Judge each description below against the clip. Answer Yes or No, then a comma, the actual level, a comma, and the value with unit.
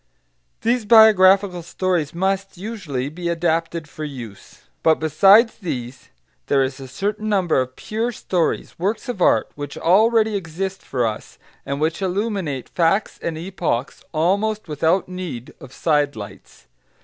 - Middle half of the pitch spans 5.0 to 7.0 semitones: Yes, average, 5.3 semitones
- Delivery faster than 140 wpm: No, slow, 135 wpm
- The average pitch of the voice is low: No, medium, 175 Hz